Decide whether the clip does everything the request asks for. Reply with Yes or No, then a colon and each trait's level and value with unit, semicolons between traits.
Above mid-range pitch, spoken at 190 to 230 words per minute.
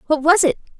Yes: very high, 310 Hz; fast, 225 wpm